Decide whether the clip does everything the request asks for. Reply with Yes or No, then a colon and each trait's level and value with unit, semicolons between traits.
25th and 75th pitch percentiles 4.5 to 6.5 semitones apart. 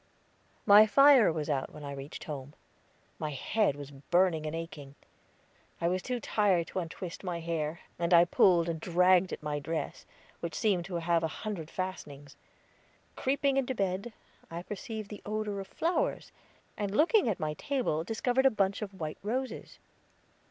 Yes: average, 5.1 semitones